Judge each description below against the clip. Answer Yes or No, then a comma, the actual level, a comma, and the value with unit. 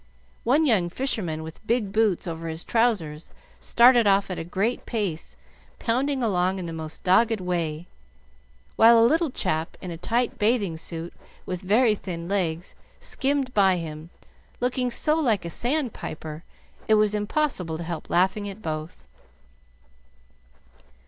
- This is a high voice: Yes, high, 195 Hz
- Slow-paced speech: No, average, 150 wpm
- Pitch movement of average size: No, wide, 5.9 semitones